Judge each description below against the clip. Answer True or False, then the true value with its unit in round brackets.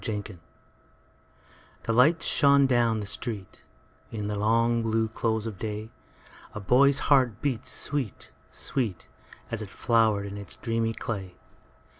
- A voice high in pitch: False (115 Hz)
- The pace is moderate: False (120 wpm)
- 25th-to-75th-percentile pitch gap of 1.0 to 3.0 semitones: True (2.4 semitones)